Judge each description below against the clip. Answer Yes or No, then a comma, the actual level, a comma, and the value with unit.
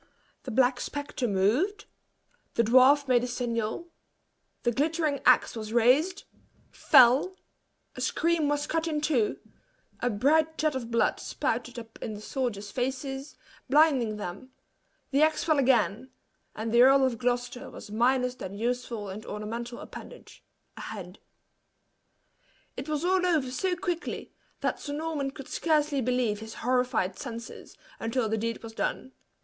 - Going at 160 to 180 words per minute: No, average, 145 wpm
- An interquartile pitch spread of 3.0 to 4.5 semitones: Yes, average, 4.2 semitones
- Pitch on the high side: Yes, very high, 255 Hz